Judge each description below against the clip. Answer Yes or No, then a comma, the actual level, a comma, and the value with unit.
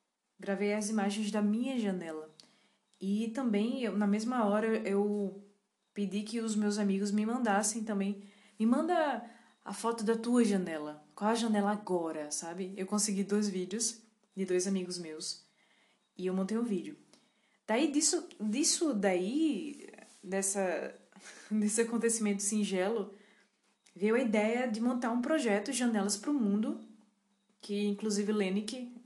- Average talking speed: Yes, average, 140 wpm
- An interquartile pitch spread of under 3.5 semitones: Yes, narrow, 2.4 semitones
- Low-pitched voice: No, high, 210 Hz